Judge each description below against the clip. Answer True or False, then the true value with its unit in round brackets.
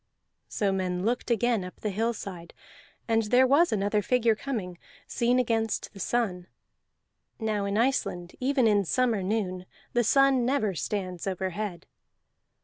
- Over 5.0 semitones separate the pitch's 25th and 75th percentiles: False (4.2 semitones)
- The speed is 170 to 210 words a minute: False (140 wpm)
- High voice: True (215 Hz)